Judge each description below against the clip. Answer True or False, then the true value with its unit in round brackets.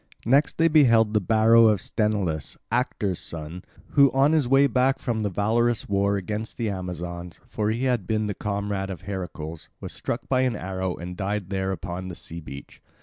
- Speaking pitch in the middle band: False (105 Hz)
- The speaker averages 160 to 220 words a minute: True (180 wpm)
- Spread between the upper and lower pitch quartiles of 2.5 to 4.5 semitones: True (4.2 semitones)